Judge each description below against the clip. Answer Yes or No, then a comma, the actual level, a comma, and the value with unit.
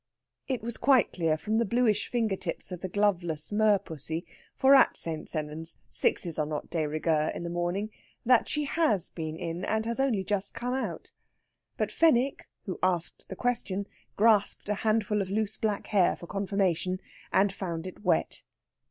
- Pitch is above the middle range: Yes, high, 195 Hz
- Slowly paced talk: No, average, 175 wpm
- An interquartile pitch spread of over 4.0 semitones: Yes, average, 4.4 semitones